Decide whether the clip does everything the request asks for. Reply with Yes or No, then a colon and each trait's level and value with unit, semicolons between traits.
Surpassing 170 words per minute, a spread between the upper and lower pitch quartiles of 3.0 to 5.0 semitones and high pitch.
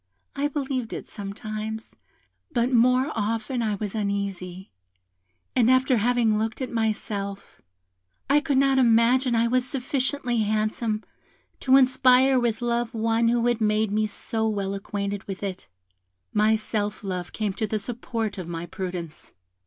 No: average, 145 wpm; average, 3.3 semitones; high, 225 Hz